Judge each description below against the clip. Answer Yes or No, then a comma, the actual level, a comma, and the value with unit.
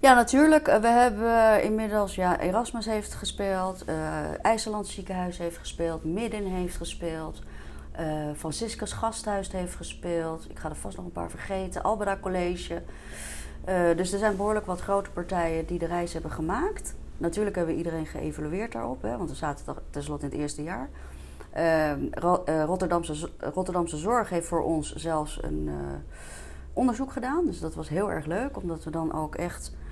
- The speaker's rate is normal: Yes, average, 165 wpm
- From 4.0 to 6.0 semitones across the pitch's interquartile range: Yes, average, 4.9 semitones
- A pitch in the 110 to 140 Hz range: No, medium, 175 Hz